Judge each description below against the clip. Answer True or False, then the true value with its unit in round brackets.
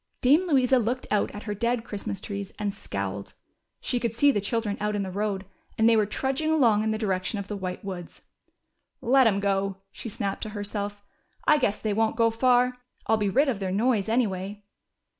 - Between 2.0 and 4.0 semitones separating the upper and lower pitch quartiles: True (3.2 semitones)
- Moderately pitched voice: False (210 Hz)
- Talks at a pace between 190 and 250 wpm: True (205 wpm)